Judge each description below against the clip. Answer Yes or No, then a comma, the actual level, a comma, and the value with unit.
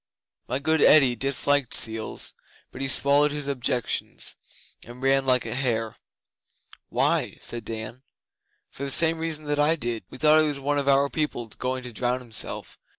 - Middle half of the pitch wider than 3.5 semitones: No, average, 3.1 semitones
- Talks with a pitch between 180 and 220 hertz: No, low, 135 Hz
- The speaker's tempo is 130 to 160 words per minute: No, average, 170 wpm